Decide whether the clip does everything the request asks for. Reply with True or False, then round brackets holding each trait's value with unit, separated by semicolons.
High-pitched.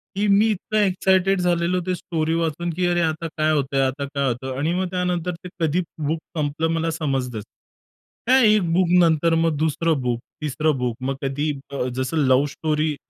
False (160 Hz)